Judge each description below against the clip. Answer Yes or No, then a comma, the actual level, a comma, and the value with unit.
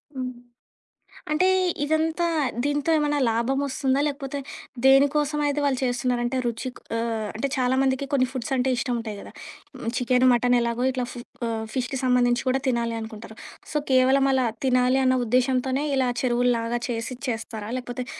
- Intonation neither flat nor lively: No, narrow, 2.1 semitones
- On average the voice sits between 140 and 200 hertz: No, very high, 255 Hz